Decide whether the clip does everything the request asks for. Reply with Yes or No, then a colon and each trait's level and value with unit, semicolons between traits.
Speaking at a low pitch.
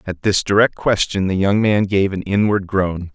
Yes: low, 100 Hz